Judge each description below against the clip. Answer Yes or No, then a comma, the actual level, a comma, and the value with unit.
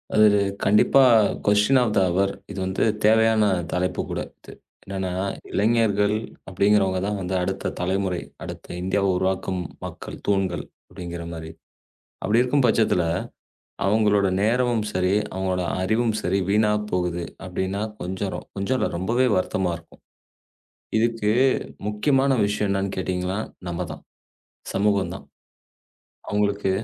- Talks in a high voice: No, low, 100 Hz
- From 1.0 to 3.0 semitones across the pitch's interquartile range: Yes, narrow, 2.4 semitones